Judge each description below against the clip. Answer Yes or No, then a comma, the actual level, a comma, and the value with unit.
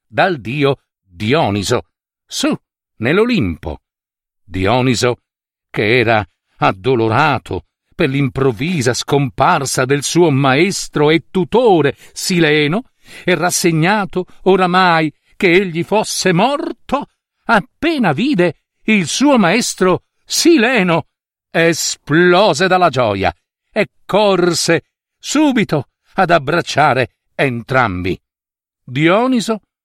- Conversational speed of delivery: No, slow, 80 wpm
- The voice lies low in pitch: No, medium, 160 Hz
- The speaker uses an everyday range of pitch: No, wide, 6.7 semitones